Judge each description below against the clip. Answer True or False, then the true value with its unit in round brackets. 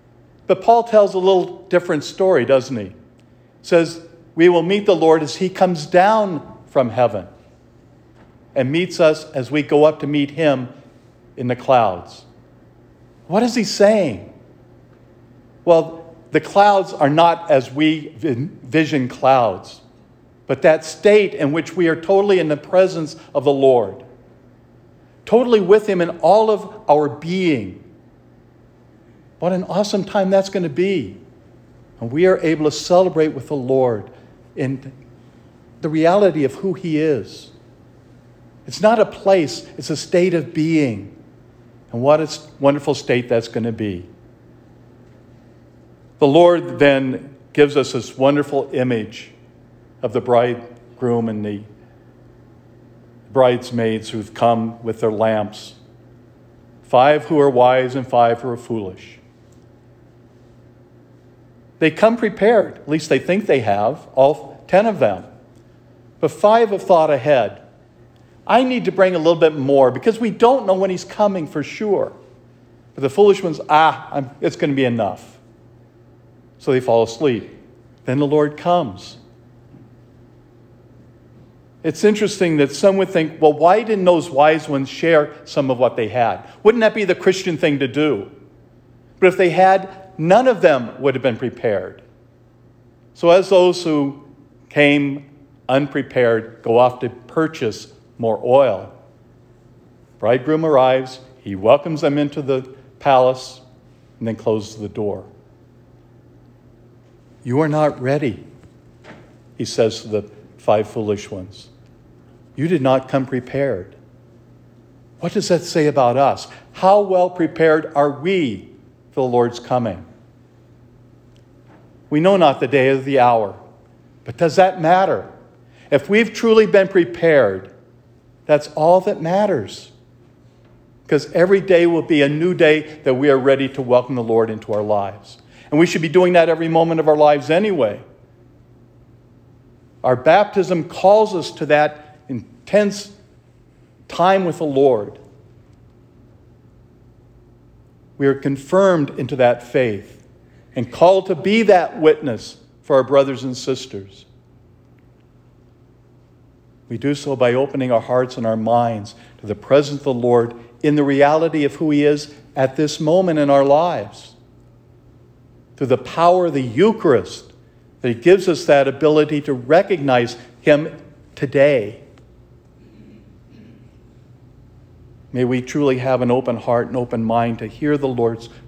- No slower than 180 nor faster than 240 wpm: False (145 wpm)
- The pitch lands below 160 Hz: True (140 Hz)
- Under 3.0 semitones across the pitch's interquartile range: False (5.4 semitones)